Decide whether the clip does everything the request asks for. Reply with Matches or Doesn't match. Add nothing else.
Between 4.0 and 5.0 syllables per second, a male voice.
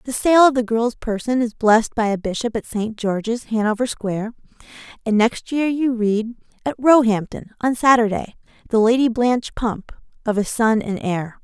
Doesn't match